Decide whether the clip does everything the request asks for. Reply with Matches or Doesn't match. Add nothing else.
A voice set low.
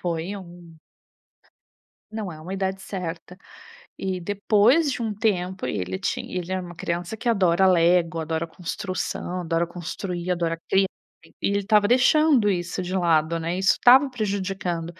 Doesn't match